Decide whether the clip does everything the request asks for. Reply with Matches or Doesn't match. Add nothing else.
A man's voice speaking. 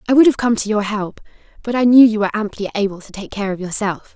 Doesn't match